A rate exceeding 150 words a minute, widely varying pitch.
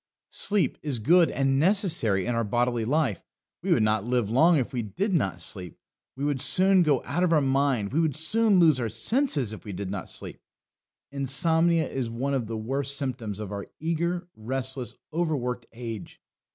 Yes: average, 190 wpm; wide, 6.0 semitones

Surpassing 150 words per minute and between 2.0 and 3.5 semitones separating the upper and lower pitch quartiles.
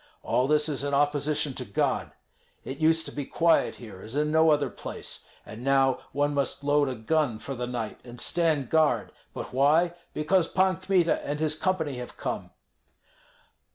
Yes: average, 180 wpm; average, 3.1 semitones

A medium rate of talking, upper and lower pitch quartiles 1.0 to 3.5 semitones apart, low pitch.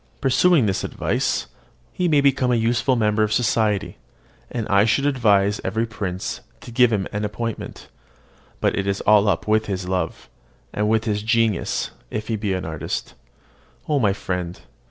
Yes: average, 170 wpm; average, 2.8 semitones; low, 110 Hz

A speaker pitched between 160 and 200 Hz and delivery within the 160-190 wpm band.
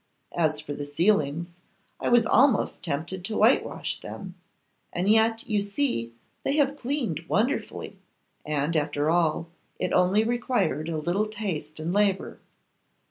No: medium, 185 Hz; slow, 135 wpm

